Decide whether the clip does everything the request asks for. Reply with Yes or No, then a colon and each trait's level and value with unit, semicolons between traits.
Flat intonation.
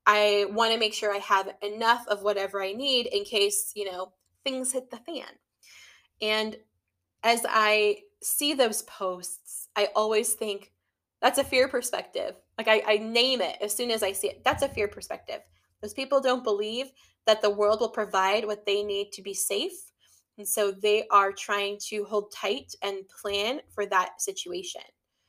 No: average, 3.2 semitones